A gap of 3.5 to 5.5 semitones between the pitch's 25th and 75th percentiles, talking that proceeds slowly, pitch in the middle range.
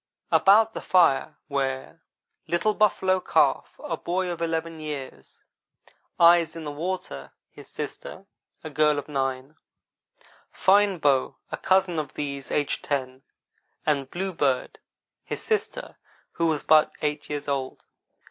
Yes: average, 4.0 semitones; slow, 130 wpm; medium, 155 Hz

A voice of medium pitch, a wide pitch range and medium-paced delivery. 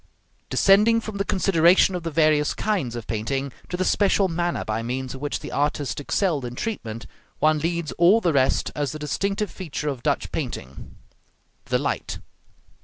Yes: medium, 155 Hz; wide, 6.0 semitones; average, 175 wpm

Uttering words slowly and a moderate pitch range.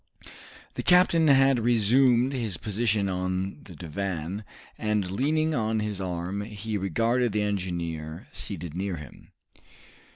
Yes: slow, 125 wpm; average, 4.5 semitones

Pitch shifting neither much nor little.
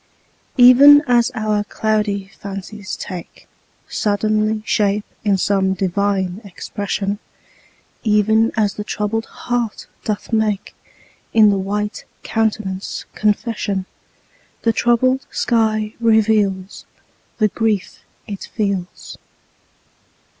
No: narrow, 1.8 semitones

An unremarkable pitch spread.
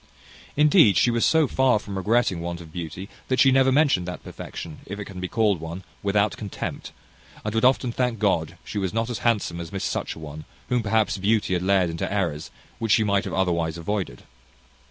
Yes: average, 4.7 semitones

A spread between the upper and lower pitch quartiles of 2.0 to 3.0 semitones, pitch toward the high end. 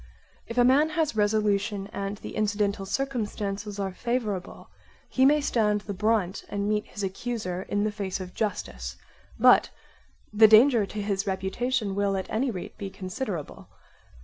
Yes: narrow, 2.6 semitones; high, 205 Hz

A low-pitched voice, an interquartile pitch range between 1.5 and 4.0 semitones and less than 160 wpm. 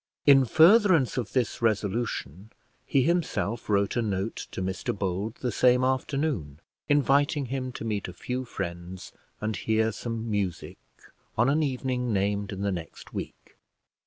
No: low, 115 Hz; average, 4.9 semitones; average, 150 wpm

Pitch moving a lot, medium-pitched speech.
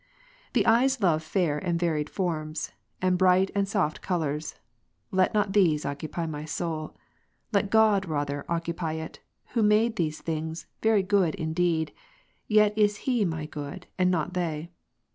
No: average, 4.2 semitones; medium, 175 Hz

